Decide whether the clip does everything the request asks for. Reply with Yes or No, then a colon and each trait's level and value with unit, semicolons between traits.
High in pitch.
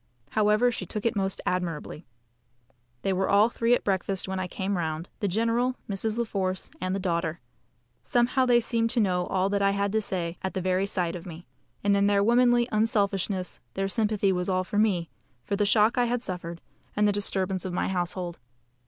Yes: high, 200 Hz